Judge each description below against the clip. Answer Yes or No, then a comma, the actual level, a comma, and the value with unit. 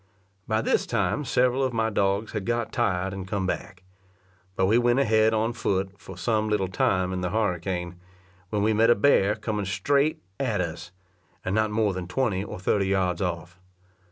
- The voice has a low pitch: Yes, low, 100 Hz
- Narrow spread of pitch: No, average, 3.2 semitones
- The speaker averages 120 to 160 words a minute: No, average, 185 wpm